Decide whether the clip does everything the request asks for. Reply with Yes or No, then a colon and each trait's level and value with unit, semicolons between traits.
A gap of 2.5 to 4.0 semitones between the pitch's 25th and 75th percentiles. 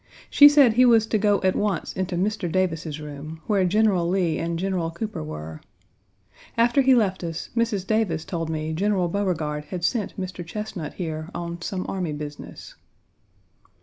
No: average, 4.4 semitones